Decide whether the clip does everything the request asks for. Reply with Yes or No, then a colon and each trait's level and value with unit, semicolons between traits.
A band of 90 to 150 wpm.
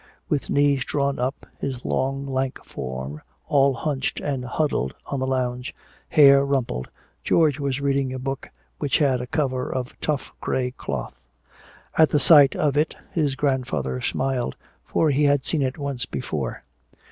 No: average, 160 wpm